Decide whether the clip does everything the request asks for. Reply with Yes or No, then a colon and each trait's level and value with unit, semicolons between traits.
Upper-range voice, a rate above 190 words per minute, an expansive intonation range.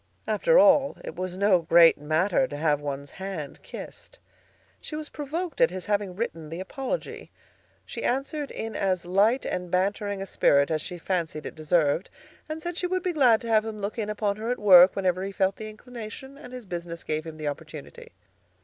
Yes: high, 195 Hz; average, 200 wpm; wide, 6.4 semitones